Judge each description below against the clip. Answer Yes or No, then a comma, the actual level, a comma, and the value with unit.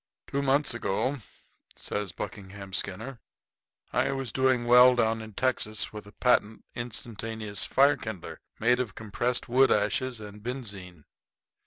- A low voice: Yes, low, 115 Hz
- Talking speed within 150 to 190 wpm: No, slow, 135 wpm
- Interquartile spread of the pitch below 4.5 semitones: Yes, average, 3.6 semitones